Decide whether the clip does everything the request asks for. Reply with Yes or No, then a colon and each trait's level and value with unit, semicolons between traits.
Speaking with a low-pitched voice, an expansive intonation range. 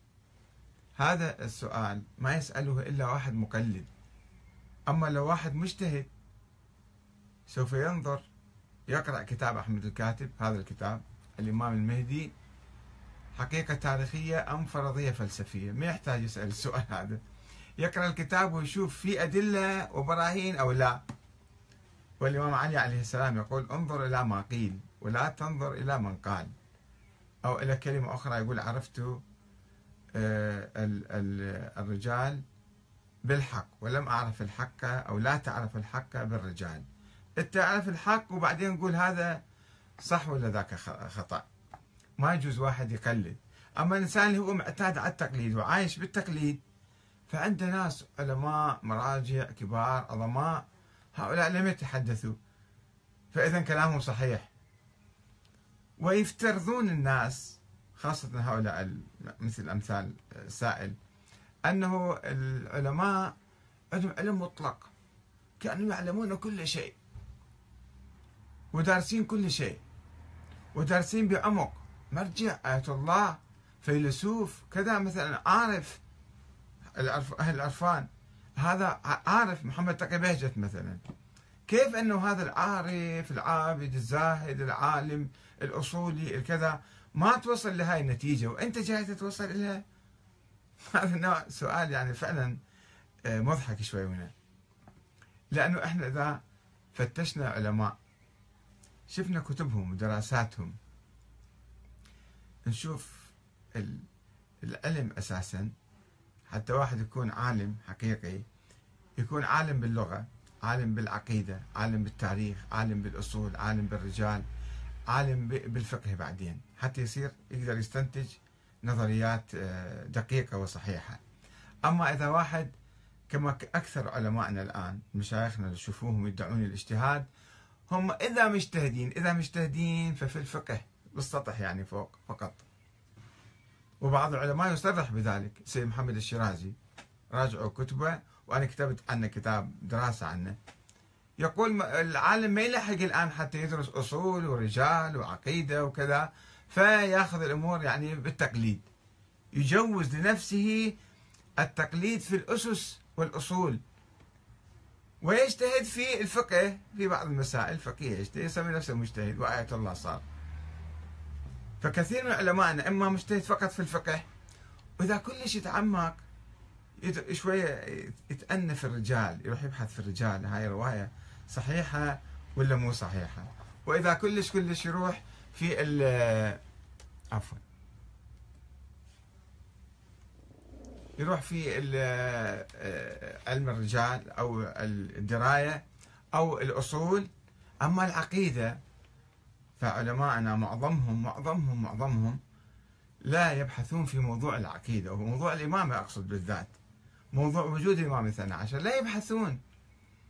Yes: low, 125 Hz; wide, 7.2 semitones